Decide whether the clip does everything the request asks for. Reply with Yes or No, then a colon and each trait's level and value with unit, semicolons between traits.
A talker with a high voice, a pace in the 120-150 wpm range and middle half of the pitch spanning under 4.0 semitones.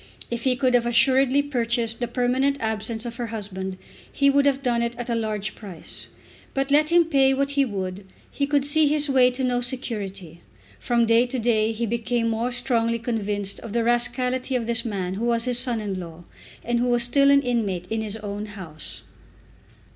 No: high, 235 Hz; average, 200 wpm; average, 3.1 semitones